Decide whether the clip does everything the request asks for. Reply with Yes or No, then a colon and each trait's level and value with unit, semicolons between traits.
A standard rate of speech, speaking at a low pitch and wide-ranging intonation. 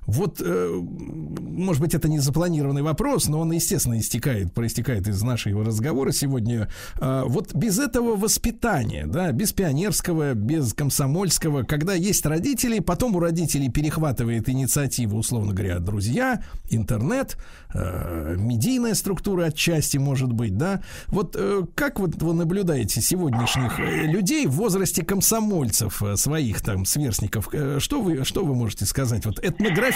No: average, 130 wpm; medium, 145 Hz; wide, 7.2 semitones